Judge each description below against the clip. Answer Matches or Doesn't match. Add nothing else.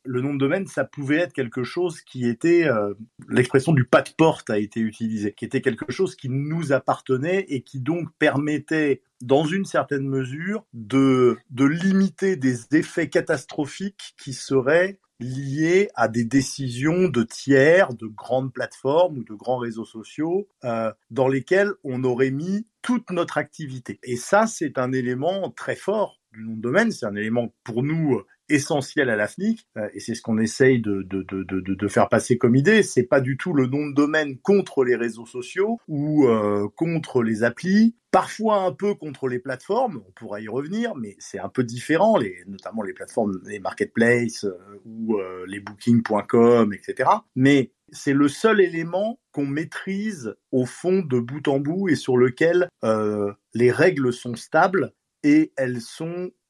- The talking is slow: Doesn't match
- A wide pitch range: Matches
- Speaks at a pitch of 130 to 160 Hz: Matches